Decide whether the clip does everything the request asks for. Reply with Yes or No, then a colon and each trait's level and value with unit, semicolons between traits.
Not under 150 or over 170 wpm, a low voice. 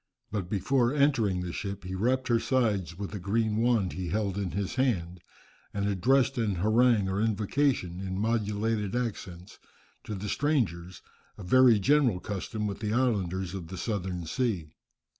Yes: average, 160 wpm; low, 105 Hz